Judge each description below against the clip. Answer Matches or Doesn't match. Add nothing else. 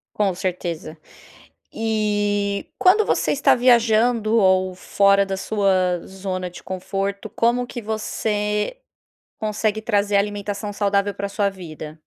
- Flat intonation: Matches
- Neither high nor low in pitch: Doesn't match